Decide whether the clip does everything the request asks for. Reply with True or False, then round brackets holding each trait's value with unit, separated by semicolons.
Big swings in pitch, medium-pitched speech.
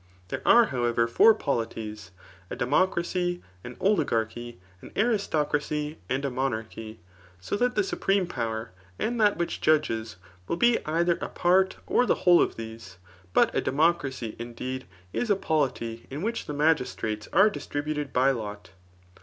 True (7.4 semitones; 145 Hz)